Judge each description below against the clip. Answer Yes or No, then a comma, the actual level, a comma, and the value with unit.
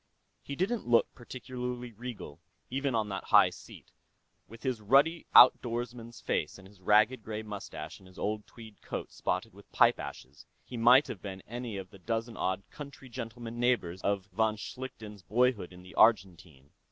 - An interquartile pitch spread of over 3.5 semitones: Yes, average, 3.9 semitones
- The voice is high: No, low, 115 Hz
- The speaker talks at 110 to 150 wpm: No, average, 170 wpm